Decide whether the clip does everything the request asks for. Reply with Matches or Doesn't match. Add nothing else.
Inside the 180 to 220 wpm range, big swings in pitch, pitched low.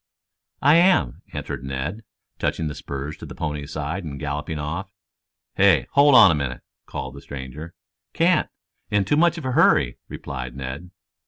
Doesn't match